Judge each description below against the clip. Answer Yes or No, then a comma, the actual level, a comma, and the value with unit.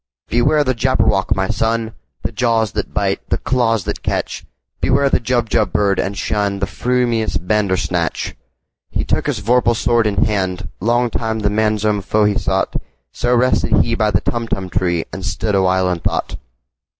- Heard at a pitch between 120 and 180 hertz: No, low, 110 Hz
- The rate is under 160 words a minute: Yes, average, 145 wpm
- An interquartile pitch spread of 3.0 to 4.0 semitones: Yes, average, 3.6 semitones